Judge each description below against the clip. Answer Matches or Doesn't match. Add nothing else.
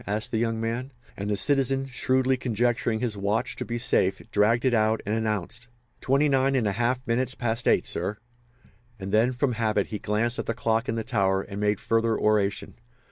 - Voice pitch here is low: Matches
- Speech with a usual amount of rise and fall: Matches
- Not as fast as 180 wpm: Doesn't match